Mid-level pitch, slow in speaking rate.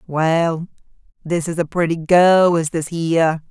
No: medium, 165 Hz; average, 155 wpm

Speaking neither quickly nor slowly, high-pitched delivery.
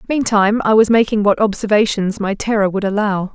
Yes: average, 180 wpm; high, 210 Hz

